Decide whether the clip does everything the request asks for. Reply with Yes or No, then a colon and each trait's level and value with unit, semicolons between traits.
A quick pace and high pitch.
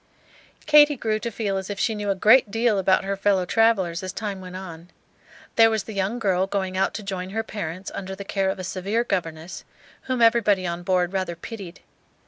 Yes: fast, 210 wpm; high, 195 Hz